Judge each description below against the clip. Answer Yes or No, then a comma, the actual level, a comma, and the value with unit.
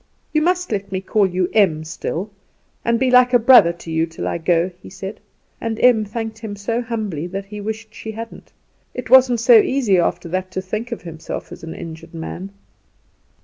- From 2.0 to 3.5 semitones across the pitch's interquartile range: No, average, 4.6 semitones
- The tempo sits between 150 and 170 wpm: No, average, 190 wpm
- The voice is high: Yes, high, 210 Hz